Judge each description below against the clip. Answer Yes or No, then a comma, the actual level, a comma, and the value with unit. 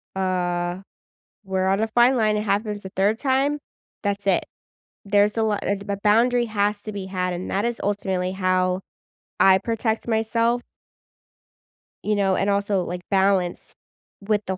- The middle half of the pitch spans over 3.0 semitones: No, narrow, 2.5 semitones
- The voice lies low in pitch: No, high, 200 Hz